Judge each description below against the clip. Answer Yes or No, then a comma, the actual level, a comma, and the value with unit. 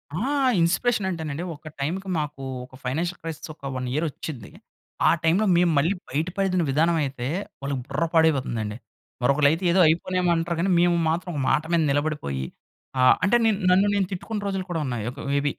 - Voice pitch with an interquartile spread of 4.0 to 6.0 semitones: Yes, average, 4.3 semitones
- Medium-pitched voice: Yes, medium, 160 Hz